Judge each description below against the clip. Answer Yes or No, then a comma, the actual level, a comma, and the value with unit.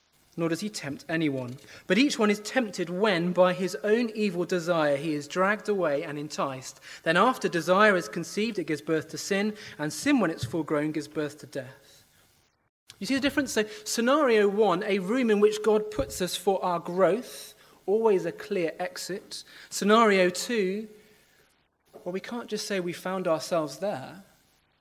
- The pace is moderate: Yes, average, 180 wpm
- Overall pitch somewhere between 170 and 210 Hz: Yes, medium, 185 Hz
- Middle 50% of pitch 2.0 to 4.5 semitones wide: No, wide, 5.5 semitones